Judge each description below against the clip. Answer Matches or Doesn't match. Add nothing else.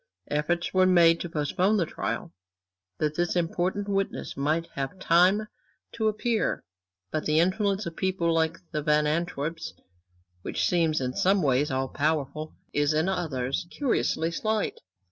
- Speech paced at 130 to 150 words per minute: Matches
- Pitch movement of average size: Matches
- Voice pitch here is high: Doesn't match